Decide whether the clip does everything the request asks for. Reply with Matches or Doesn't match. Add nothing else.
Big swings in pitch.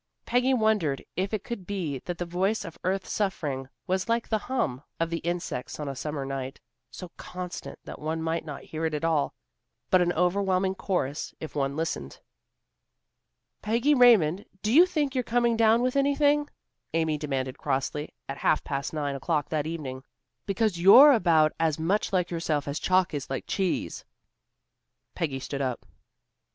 Matches